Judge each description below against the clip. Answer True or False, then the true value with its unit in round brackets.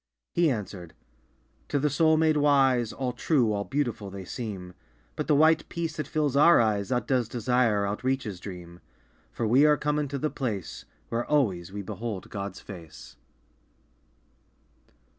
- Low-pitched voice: True (120 Hz)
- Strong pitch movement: True (6.4 semitones)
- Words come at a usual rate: True (150 wpm)